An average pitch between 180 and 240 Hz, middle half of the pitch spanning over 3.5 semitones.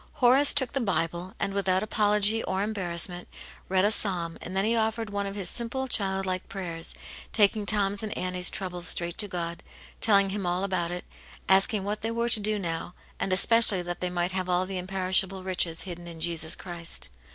No: high, 190 Hz; average, 2.8 semitones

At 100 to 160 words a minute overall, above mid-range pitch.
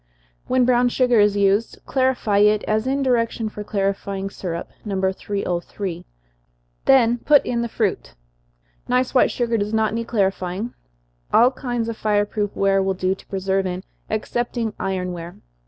Yes: average, 155 wpm; high, 210 Hz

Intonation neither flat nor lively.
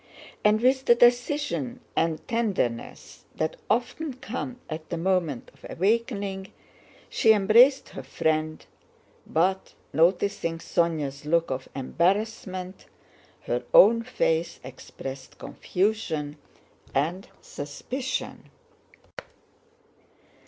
No: wide, 6.7 semitones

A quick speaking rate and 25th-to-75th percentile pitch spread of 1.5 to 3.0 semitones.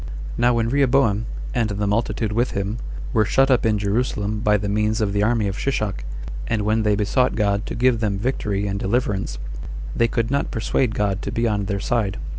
Yes: fast, 210 wpm; narrow, 2.4 semitones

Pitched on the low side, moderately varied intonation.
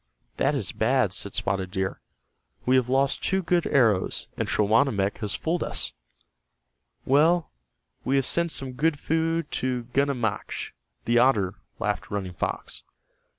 No: low, 130 Hz; wide, 6.3 semitones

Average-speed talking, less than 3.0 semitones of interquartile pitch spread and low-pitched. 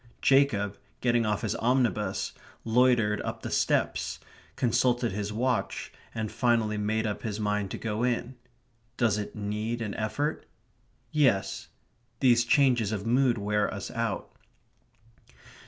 No: slow, 130 wpm; narrow, 2.6 semitones; low, 115 Hz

